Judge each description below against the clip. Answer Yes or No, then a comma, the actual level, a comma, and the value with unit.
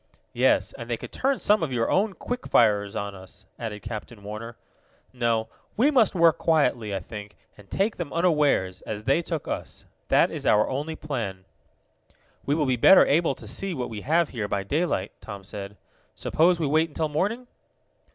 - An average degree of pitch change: No, wide, 8.1 semitones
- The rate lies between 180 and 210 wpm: Yes, average, 185 wpm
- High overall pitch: No, low, 130 Hz